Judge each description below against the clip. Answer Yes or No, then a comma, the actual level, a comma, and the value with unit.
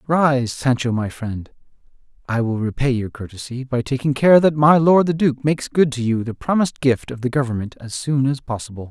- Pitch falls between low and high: No, low, 130 Hz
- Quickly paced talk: Yes, fast, 210 wpm